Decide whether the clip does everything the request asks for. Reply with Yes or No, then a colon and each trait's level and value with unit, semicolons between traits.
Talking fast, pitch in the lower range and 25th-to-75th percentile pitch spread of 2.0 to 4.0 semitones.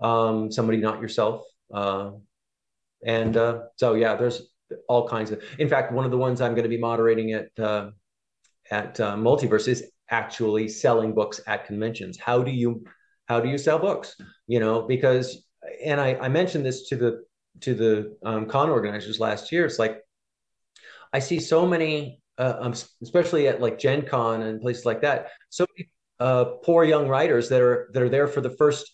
No: average, 190 wpm; low, 120 Hz; average, 3.7 semitones